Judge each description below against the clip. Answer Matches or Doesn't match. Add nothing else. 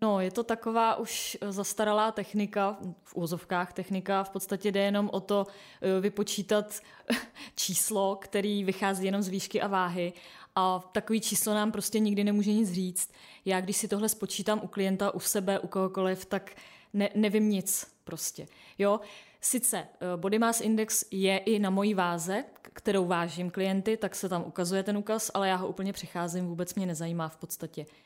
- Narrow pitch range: Matches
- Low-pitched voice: Doesn't match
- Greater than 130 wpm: Matches